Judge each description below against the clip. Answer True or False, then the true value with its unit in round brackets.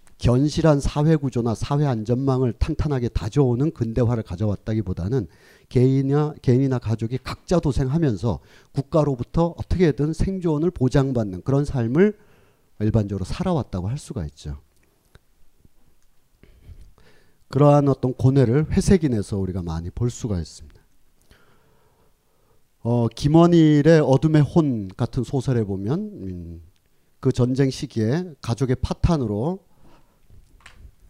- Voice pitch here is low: True (130 Hz)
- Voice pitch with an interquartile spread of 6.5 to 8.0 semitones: False (5.5 semitones)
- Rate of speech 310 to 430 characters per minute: False (275 characters per minute)